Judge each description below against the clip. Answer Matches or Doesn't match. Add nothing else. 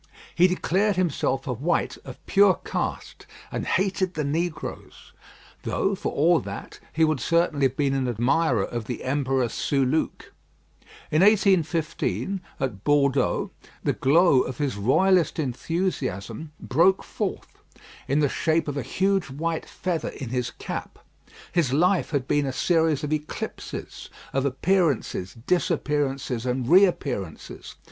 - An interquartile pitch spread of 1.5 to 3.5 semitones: Doesn't match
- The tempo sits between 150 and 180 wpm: Doesn't match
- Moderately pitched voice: Matches